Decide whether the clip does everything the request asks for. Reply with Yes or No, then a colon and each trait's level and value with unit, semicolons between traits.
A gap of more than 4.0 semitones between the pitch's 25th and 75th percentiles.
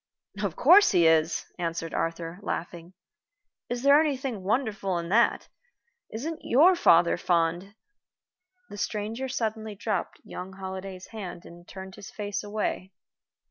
Yes: average, 5.3 semitones